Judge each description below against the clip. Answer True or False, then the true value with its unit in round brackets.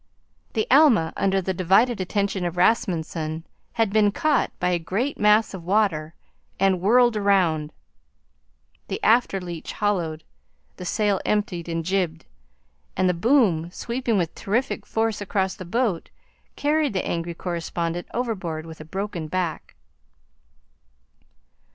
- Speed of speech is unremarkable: False (130 wpm)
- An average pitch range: True (4.2 semitones)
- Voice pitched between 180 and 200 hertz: True (190 Hz)